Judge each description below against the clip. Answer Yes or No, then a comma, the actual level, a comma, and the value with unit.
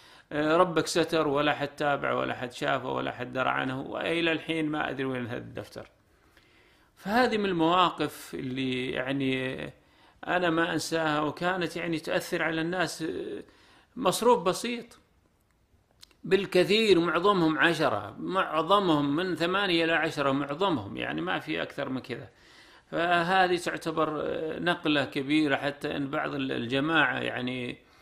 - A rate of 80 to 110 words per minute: No, average, 125 wpm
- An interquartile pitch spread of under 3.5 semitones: No, average, 4.2 semitones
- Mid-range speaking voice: Yes, medium, 160 Hz